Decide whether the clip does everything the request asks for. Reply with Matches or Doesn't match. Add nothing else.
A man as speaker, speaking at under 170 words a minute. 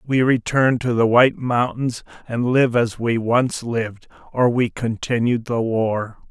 Matches